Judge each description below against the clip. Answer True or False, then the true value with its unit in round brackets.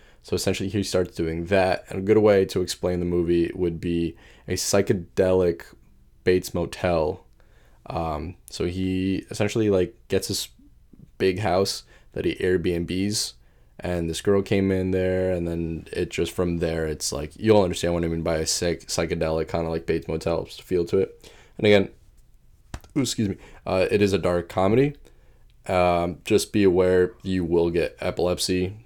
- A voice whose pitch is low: True (90 Hz)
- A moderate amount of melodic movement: False (2.2 semitones)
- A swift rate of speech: False (170 wpm)